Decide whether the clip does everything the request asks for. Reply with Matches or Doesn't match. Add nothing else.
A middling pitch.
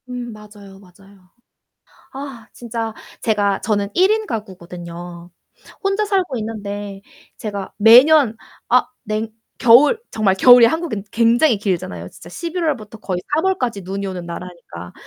Doesn't match